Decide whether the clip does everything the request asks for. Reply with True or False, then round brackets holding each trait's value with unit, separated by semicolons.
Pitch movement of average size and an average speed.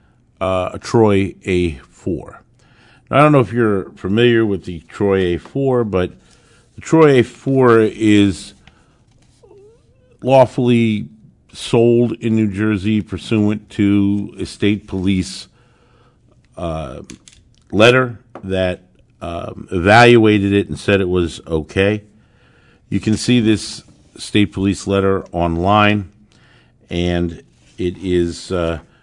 False (4.1 semitones; 110 wpm)